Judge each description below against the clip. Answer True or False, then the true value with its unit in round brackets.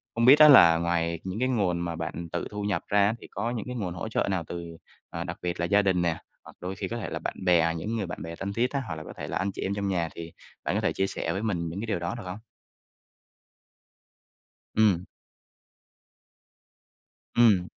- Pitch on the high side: False (95 Hz)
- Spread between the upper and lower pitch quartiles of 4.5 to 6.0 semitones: False (4.0 semitones)